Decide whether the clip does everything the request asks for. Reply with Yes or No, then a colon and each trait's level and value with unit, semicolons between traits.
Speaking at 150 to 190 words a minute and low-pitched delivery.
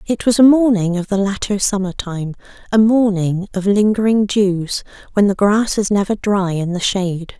No: average, 185 wpm; high, 200 Hz